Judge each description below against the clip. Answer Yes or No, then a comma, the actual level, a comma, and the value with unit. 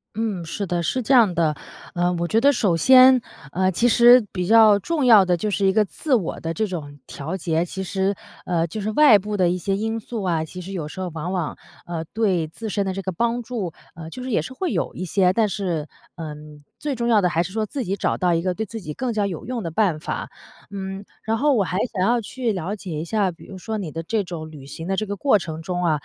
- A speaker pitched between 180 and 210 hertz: Yes, high, 190 Hz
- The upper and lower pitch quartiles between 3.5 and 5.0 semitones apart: Yes, average, 4.5 semitones